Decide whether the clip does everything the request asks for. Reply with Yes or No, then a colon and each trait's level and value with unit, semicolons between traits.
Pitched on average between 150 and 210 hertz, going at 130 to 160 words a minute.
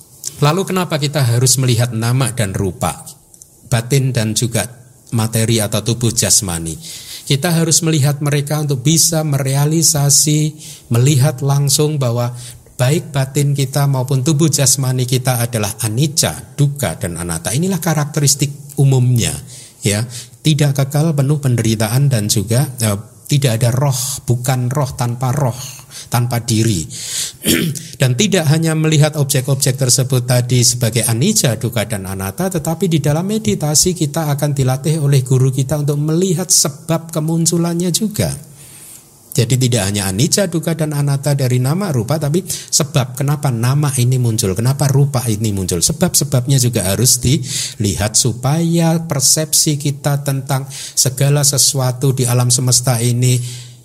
No: low, 135 Hz; average, 135 wpm